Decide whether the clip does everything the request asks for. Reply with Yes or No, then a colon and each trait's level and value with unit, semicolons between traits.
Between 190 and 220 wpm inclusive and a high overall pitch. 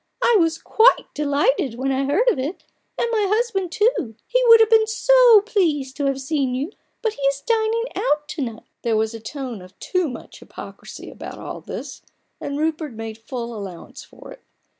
Yes: average, 195 wpm; very high, 295 Hz